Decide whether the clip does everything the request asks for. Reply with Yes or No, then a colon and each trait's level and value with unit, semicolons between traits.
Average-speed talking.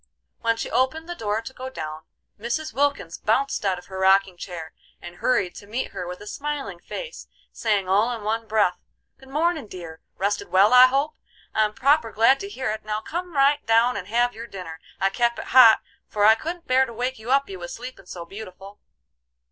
No: fast, 210 wpm